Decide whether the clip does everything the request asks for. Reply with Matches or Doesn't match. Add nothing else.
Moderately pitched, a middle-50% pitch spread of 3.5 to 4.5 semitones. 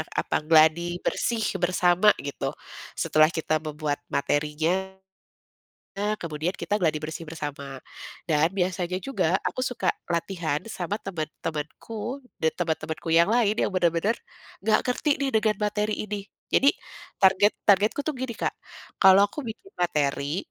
Doesn't match